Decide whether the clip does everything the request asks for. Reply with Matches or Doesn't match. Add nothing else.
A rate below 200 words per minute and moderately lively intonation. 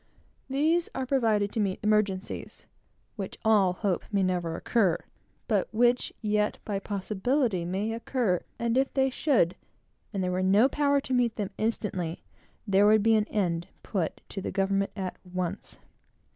Matches